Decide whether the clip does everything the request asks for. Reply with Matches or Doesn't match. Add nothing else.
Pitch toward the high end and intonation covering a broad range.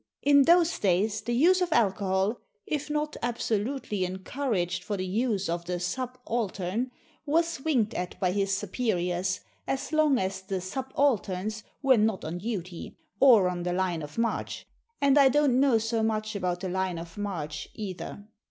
Matches